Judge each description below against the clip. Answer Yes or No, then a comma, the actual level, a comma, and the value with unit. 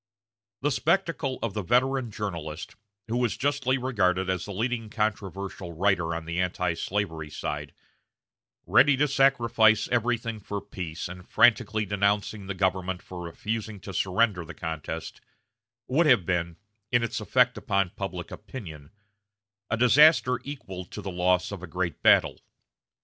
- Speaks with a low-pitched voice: Yes, low, 100 Hz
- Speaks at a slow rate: No, average, 145 wpm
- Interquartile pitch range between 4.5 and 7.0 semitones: Yes, average, 5.1 semitones